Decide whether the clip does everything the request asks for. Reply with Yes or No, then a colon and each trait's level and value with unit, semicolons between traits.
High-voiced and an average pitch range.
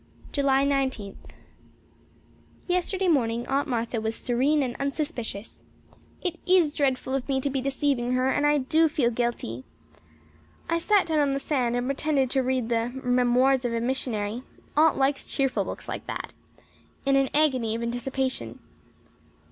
Yes: very high, 265 Hz; average, 3.0 semitones